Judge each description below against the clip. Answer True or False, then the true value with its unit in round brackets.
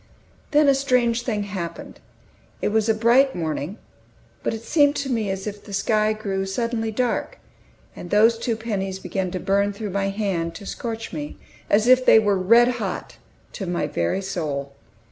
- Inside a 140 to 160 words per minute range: False (180 wpm)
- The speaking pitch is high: True (210 Hz)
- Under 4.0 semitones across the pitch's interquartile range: True (3.3 semitones)